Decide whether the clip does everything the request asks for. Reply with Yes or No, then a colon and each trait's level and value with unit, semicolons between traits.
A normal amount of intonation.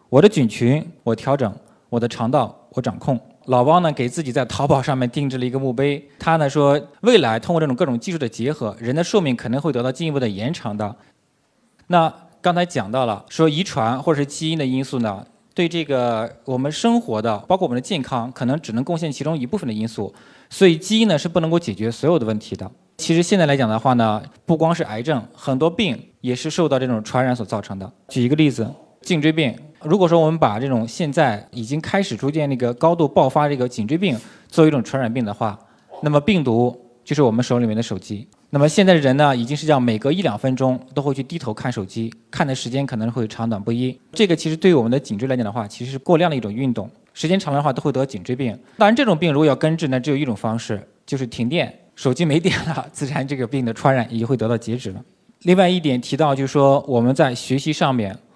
Yes: average, 5.0 semitones